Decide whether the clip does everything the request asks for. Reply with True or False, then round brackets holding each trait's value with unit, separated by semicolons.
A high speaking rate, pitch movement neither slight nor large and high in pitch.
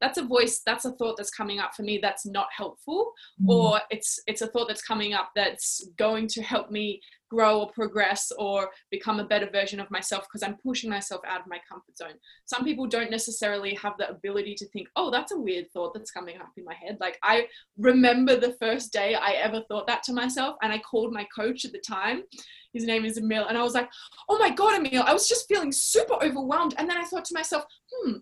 True (235 wpm; 3.9 semitones; 220 Hz)